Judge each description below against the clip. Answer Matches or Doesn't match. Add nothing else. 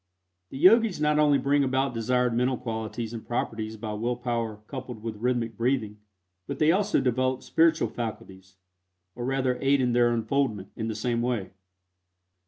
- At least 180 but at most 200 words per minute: Doesn't match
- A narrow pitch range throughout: Doesn't match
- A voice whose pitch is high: Doesn't match